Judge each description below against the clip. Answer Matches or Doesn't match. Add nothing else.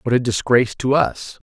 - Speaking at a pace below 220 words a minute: Matches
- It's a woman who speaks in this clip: Doesn't match